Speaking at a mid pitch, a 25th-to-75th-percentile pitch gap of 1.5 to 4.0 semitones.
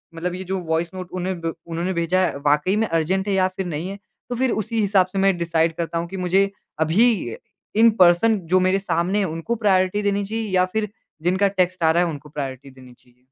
Yes: medium, 180 Hz; average, 2.9 semitones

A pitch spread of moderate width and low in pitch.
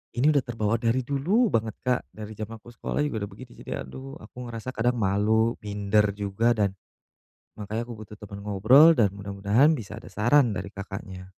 Yes: average, 3.3 semitones; low, 110 Hz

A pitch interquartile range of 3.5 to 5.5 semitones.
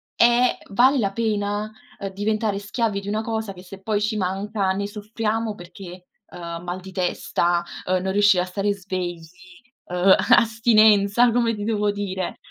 No: average, 2.7 semitones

